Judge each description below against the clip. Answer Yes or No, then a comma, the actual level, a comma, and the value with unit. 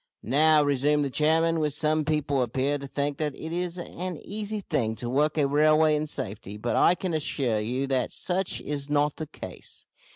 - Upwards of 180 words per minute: Yes, average, 190 wpm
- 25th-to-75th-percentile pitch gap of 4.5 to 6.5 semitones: No, narrow, 2.5 semitones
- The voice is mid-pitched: Yes, medium, 150 Hz